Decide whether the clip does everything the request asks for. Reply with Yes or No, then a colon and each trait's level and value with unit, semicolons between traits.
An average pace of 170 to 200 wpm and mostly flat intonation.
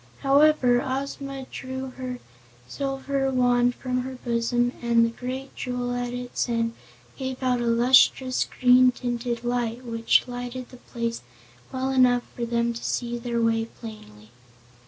No: average, 145 wpm; narrow, 1.6 semitones